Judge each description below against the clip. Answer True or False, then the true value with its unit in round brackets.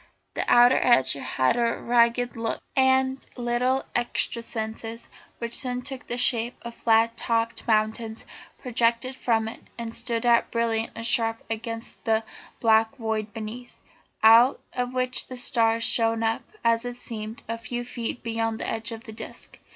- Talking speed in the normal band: True (160 wpm)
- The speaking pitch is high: True (230 Hz)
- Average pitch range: False (1.3 semitones)